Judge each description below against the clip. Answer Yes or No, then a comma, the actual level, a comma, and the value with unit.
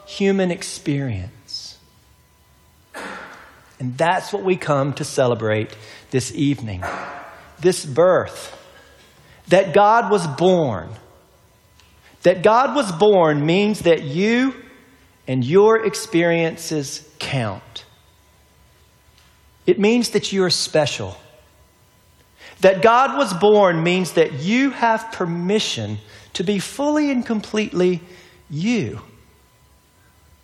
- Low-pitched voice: No, medium, 165 Hz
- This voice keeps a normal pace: No, slow, 95 wpm